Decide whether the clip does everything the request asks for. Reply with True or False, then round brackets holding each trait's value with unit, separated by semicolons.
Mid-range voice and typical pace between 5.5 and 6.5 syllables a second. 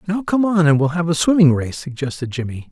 True (155 Hz; 5.9 syllables/s)